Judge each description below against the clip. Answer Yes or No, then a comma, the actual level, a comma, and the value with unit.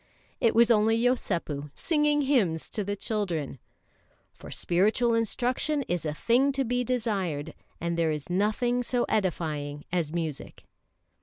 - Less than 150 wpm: Yes, average, 140 wpm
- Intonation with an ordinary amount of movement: No, wide, 6.8 semitones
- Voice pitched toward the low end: No, high, 210 Hz